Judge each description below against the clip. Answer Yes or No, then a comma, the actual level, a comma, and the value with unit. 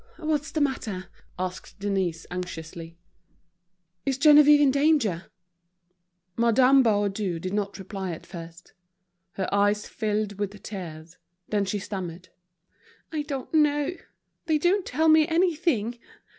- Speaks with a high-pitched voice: Yes, high, 210 Hz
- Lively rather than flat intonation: Yes, wide, 7.9 semitones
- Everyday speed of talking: No, slow, 120 wpm